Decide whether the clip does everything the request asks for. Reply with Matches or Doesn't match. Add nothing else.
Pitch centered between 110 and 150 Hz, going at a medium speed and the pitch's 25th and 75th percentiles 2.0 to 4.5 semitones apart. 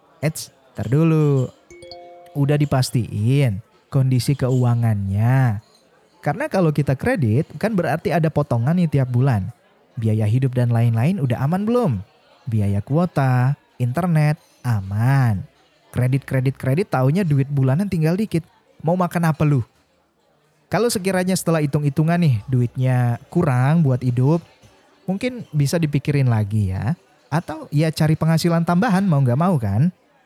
Doesn't match